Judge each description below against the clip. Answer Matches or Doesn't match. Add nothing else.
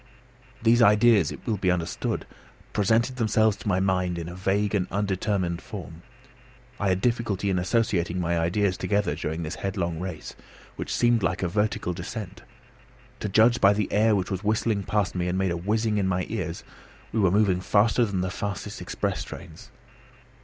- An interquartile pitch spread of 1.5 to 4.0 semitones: Matches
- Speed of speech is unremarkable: Matches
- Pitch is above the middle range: Doesn't match